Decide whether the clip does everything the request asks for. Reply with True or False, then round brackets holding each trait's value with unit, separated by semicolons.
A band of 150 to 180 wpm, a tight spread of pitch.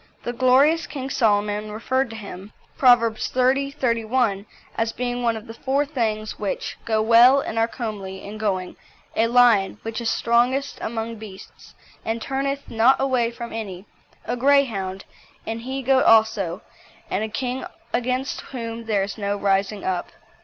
False (160 wpm; 3.1 semitones)